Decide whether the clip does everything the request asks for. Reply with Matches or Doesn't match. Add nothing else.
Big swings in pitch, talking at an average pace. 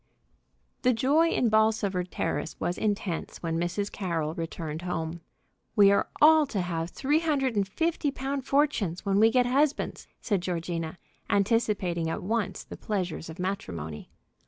Matches